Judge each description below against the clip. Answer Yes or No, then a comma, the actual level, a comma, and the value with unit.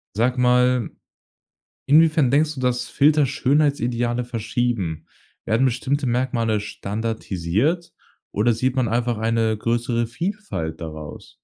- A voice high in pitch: No, low, 120 Hz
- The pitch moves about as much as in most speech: Yes, average, 3.0 semitones